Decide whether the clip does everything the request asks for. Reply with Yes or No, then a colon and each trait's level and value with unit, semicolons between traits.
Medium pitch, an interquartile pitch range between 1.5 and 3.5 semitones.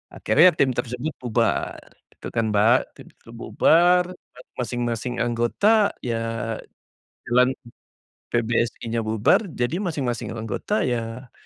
No: low, 120 Hz; narrow, 2.4 semitones